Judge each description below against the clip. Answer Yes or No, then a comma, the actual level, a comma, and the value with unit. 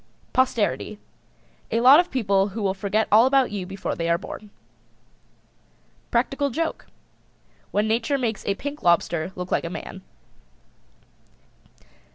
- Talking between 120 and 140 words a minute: Yes, slow, 135 wpm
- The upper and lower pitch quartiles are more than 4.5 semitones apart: Yes, average, 5.1 semitones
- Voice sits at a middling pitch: No, high, 215 Hz